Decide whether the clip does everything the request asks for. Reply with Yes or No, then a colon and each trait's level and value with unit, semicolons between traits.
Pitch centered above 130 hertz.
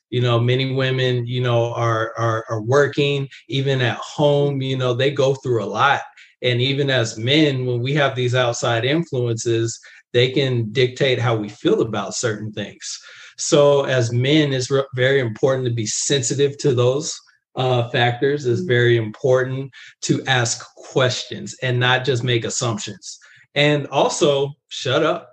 No: low, 125 Hz